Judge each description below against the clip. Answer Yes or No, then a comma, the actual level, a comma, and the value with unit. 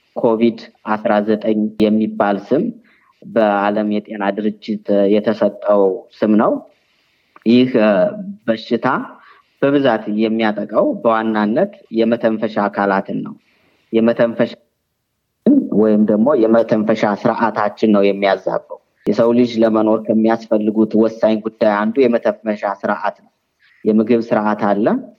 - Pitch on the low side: Yes, low, 110 Hz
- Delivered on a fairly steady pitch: Yes, narrow, 1.6 semitones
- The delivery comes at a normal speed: Yes, average, 95 wpm